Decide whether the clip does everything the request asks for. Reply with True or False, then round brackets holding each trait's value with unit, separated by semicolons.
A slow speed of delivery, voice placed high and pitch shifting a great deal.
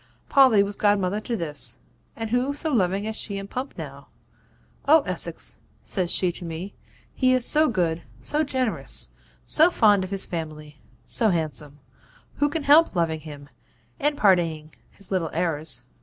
False (160 wpm; 195 Hz; 7.6 semitones)